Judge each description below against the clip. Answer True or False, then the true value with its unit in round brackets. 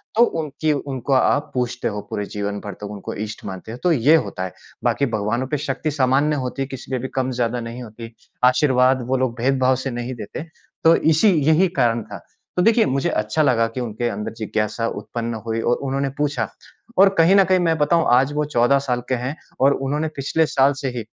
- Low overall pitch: True (130 Hz)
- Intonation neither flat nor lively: True (4.0 semitones)